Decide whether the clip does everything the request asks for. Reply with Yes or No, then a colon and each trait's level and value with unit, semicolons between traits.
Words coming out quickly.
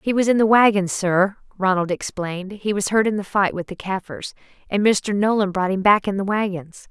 Yes: fast, 225 wpm